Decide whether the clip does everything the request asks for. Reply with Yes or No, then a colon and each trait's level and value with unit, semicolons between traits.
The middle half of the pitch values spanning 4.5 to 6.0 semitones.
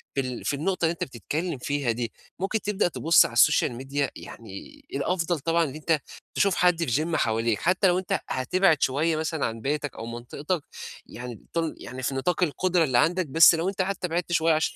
Yes: average, 5.3 semitones